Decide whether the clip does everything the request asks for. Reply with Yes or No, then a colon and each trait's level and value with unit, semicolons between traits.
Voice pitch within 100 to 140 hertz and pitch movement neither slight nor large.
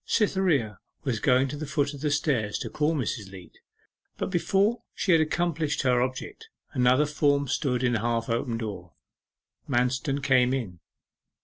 Yes: low, 135 Hz; average, 4.1 semitones